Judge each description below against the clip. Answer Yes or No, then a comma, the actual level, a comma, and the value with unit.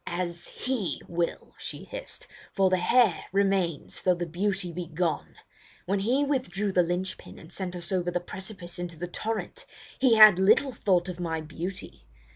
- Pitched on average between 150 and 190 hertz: Yes, medium, 185 Hz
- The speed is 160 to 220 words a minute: Yes, average, 175 wpm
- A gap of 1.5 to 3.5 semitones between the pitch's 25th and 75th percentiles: Yes, average, 2.7 semitones